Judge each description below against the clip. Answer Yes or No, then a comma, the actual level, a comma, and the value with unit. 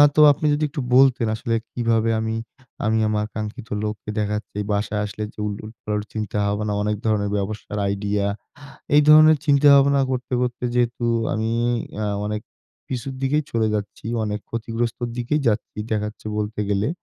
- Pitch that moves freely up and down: No, average, 2.8 semitones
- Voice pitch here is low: Yes, low, 110 Hz